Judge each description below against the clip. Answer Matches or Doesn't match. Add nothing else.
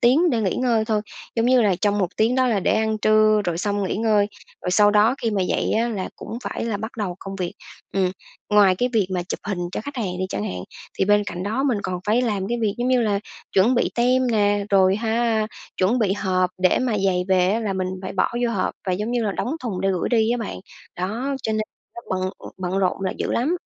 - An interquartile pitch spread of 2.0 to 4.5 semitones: Matches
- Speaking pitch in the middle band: Doesn't match